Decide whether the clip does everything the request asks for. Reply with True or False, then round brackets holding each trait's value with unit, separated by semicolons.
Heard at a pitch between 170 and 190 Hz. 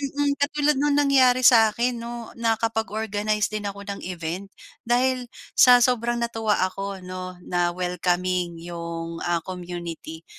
False (210 Hz)